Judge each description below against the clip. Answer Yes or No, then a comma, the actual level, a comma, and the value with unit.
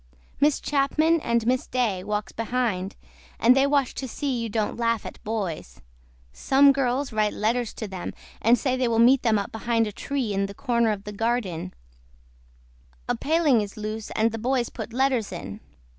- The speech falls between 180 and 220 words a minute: Yes, average, 185 wpm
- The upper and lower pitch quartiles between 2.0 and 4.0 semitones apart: Yes, average, 3.5 semitones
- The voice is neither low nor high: No, high, 230 Hz